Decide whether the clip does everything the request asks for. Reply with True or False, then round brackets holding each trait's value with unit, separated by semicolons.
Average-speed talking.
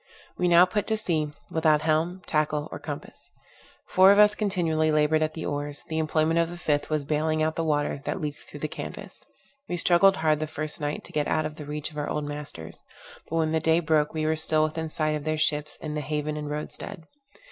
False (235 wpm)